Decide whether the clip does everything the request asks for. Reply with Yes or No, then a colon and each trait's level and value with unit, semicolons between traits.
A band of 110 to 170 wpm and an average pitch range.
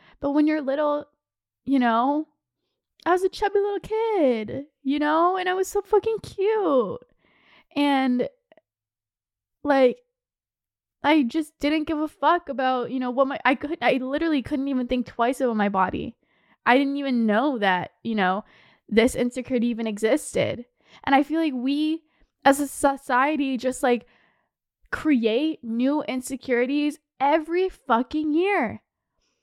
Yes: average, 145 wpm; average, 3.9 semitones